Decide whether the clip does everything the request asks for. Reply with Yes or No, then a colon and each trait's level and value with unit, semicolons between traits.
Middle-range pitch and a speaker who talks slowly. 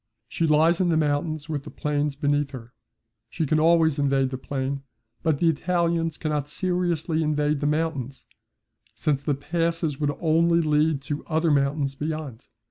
No: medium, 150 Hz; average, 160 wpm